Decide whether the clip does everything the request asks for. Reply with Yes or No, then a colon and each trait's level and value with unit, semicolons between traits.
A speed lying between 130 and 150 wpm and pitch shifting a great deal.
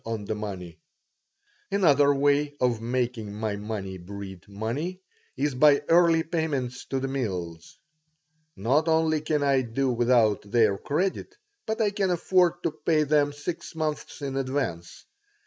Yes: average, 145 wpm; wide, 6.2 semitones